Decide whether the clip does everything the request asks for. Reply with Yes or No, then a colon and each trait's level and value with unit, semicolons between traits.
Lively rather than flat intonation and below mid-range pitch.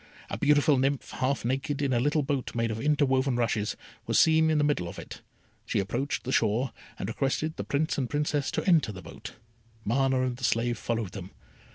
No: average, 3.8 semitones; low, 130 Hz